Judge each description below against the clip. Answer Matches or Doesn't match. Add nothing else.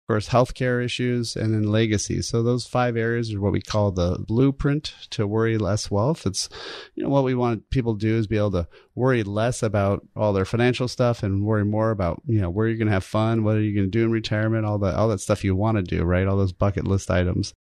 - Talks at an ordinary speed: Doesn't match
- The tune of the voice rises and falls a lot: Doesn't match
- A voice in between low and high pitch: Doesn't match